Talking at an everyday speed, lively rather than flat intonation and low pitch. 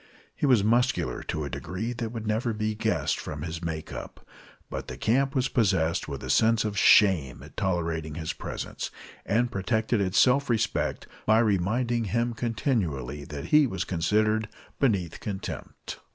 Yes: average, 165 wpm; wide, 5.7 semitones; low, 105 Hz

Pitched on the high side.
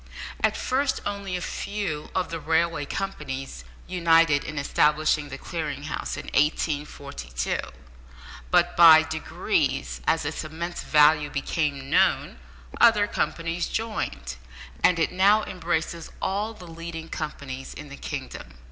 No: medium, 160 Hz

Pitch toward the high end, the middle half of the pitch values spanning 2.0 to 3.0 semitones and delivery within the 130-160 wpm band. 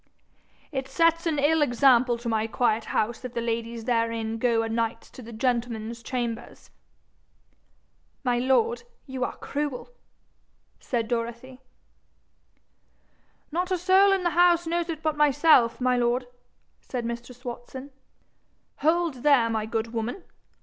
No: very high, 250 Hz; average, 4.3 semitones; slow, 135 wpm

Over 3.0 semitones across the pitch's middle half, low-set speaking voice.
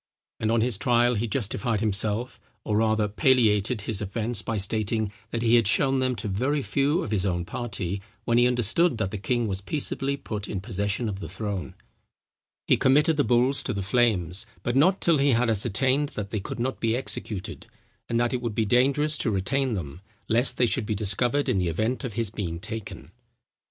Yes: average, 3.8 semitones; low, 115 Hz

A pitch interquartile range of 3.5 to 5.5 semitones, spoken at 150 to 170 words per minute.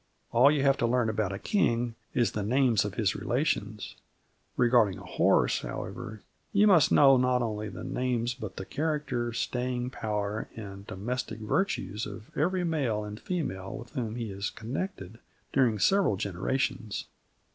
Yes: average, 3.8 semitones; average, 155 wpm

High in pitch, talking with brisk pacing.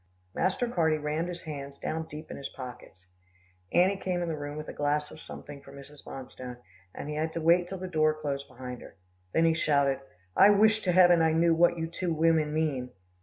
No: medium, 155 Hz; fast, 220 wpm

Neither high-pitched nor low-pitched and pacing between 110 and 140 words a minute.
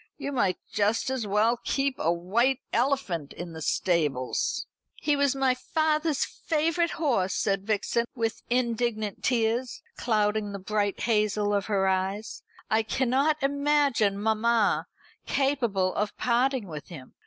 No: high, 225 Hz; slow, 135 wpm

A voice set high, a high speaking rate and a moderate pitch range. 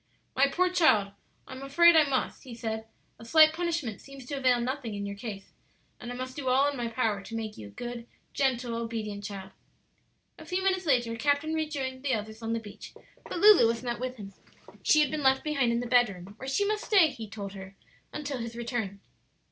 Yes: high, 245 Hz; fast, 220 wpm; average, 4.4 semitones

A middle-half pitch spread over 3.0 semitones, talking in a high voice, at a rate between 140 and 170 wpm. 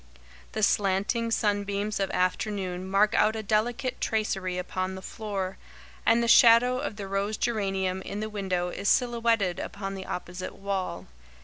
No: narrow, 2.5 semitones; high, 200 Hz; average, 150 wpm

